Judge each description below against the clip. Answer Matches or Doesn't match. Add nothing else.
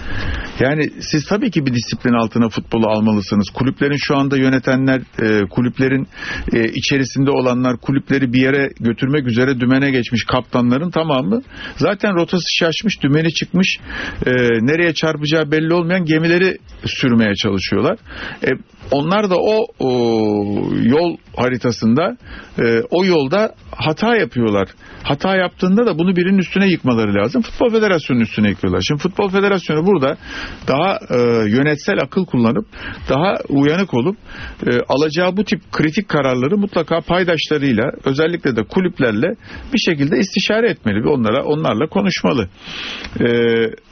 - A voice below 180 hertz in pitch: Matches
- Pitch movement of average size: Doesn't match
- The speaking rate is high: Doesn't match